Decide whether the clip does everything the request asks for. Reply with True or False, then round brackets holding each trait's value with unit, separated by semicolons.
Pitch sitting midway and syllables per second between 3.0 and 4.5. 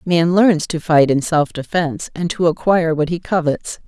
False (165 Hz; 4.9 syllables/s)